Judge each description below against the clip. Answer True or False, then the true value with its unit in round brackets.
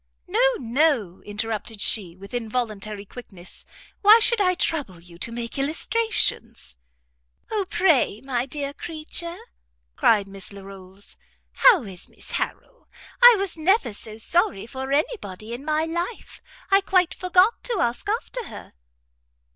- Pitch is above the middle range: True (260 Hz)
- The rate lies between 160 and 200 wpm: False (140 wpm)